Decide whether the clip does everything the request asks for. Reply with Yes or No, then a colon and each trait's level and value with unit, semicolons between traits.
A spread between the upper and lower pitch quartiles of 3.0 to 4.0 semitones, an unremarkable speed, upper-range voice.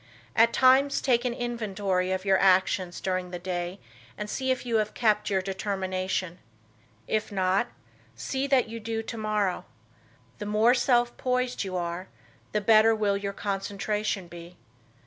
Yes: average, 3.6 semitones; average, 150 wpm; high, 205 Hz